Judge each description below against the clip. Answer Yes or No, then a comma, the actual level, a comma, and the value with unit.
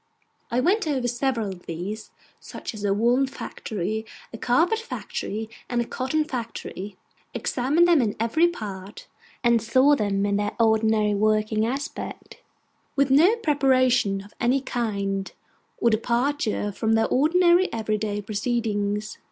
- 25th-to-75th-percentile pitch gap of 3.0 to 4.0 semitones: No, average, 4.4 semitones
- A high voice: Yes, high, 230 Hz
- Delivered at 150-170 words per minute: No, slow, 135 wpm